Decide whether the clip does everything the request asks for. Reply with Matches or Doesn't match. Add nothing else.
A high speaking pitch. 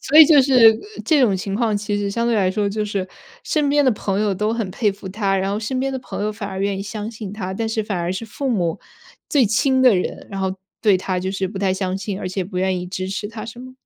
Matches